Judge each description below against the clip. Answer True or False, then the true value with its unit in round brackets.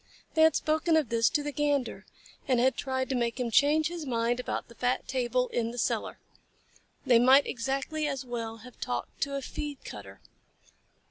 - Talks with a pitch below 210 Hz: False (260 Hz)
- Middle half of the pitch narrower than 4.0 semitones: True (3.4 semitones)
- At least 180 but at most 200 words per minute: True (190 wpm)